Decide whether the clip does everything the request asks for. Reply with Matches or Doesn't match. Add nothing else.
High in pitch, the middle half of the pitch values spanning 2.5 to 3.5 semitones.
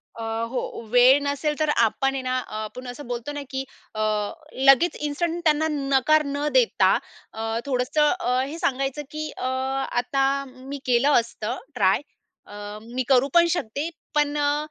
Matches